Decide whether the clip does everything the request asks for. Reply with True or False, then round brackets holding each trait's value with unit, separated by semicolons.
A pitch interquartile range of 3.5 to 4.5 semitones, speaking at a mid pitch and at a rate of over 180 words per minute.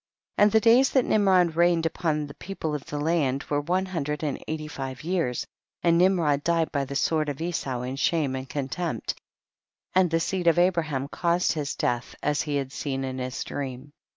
True (3.9 semitones; 155 Hz; 200 wpm)